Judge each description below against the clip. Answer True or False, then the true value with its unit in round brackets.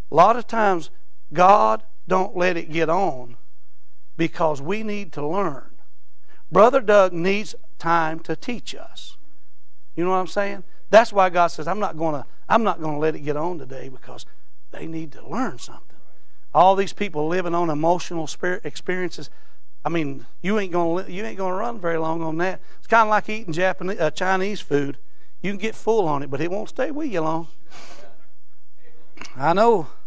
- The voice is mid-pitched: True (170 Hz)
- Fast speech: False (180 wpm)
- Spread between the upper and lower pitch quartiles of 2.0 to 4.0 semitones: False (4.5 semitones)